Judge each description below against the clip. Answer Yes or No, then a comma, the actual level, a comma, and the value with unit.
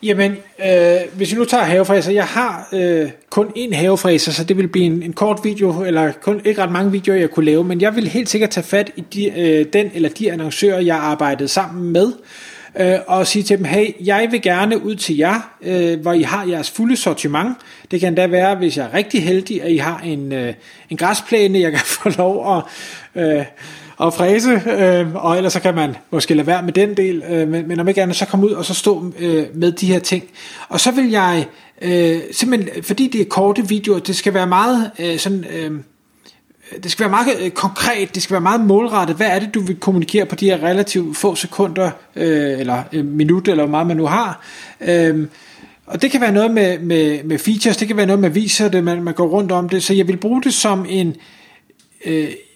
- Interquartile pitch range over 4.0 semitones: No, average, 3.3 semitones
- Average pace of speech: No, fast, 230 wpm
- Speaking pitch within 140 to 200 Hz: Yes, medium, 185 Hz